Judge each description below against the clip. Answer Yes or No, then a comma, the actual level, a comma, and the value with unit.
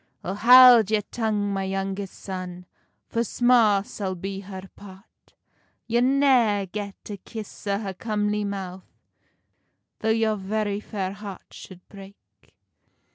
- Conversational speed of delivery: No, slow, 130 wpm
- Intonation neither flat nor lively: No, narrow, 2.2 semitones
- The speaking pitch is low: No, high, 205 Hz